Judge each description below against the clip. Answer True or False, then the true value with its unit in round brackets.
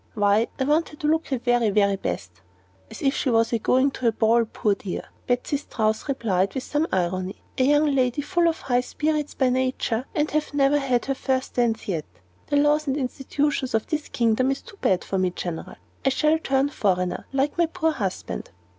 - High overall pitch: True (255 Hz)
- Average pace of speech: False (210 wpm)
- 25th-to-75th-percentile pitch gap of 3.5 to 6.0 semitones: True (5.0 semitones)